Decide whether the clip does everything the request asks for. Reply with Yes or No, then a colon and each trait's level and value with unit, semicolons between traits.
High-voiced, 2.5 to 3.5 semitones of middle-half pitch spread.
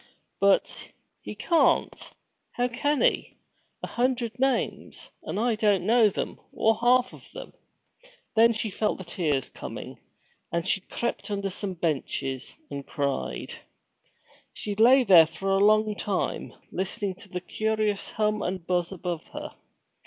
No: high, 205 Hz; average, 4.1 semitones